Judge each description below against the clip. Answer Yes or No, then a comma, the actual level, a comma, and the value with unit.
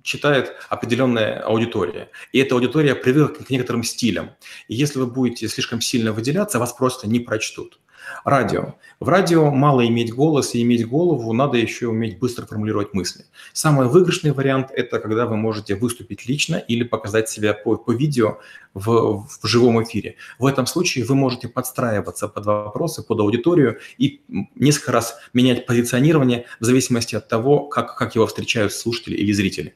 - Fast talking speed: Yes, fast, 165 wpm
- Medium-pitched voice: No, low, 120 Hz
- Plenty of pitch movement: No, average, 3.2 semitones